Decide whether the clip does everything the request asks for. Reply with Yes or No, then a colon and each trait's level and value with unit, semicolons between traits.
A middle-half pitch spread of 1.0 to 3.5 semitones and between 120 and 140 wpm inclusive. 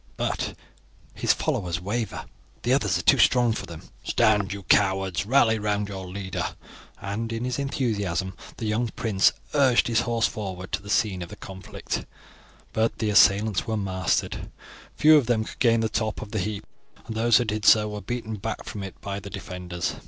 No: average, 3.0 semitones; average, 185 wpm